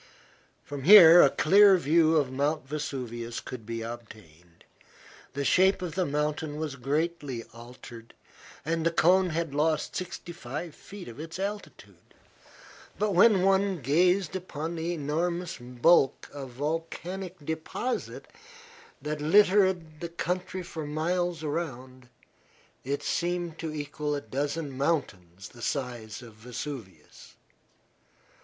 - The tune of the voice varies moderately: Yes, average, 4.7 semitones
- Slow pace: Yes, slow, 125 wpm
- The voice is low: No, medium, 155 Hz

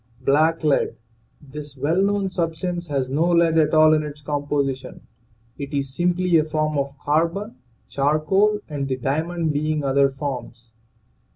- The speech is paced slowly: No, average, 150 wpm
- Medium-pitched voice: Yes, medium, 150 Hz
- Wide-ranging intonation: No, average, 3.0 semitones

